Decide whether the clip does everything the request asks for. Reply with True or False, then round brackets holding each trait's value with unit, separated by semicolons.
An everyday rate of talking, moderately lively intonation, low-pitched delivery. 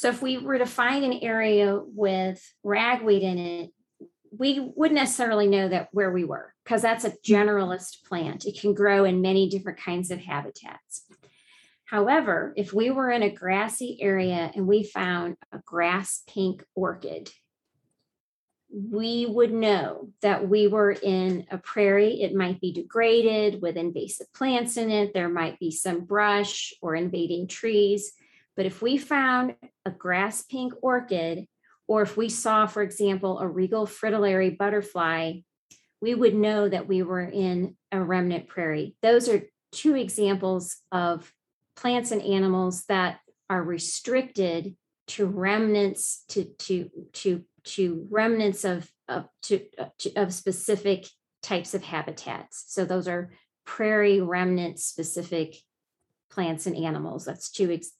False (145 wpm; 3.1 semitones; 195 Hz)